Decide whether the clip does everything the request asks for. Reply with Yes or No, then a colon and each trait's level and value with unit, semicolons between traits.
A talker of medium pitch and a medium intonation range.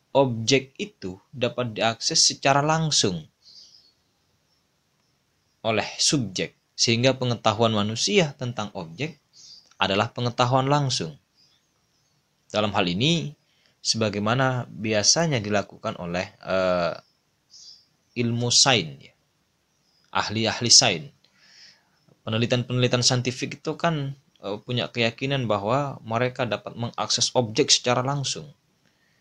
No: low, 125 Hz; average, 4.3 semitones